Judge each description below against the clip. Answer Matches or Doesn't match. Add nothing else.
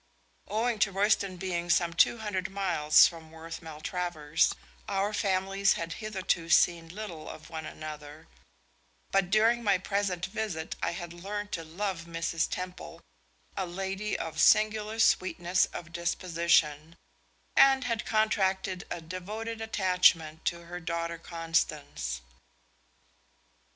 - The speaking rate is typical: Doesn't match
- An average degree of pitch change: Matches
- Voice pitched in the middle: Matches